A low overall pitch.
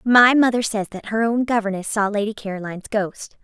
No: high, 215 Hz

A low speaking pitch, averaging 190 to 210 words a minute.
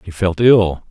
Yes: very low, 95 Hz; average, 200 wpm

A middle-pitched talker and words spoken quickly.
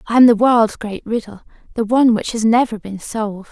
No: high, 220 Hz; fast, 220 wpm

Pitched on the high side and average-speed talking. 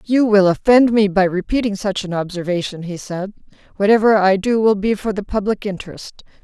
Yes: high, 200 Hz; average, 185 wpm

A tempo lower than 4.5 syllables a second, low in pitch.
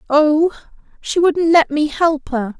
No: 3.7 syllables/s; very high, 305 Hz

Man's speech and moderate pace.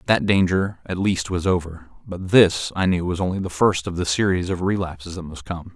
No: male; fast, 230 wpm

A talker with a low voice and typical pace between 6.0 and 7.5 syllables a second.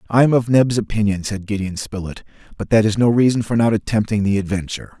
Yes: low, 105 Hz; 6.3 syllables/s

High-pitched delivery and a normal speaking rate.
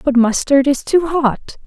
Yes: very high, 280 Hz; average, 180 wpm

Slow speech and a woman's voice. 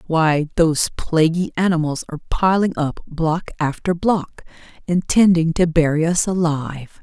Yes: slow, 130 wpm; female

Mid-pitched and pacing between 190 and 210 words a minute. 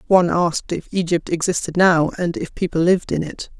Yes: medium, 175 Hz; average, 200 wpm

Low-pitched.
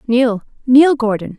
No: high, 240 Hz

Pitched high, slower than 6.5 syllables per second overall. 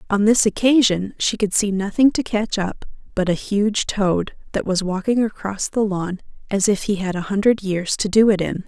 Yes: high, 205 Hz; 4.8 syllables/s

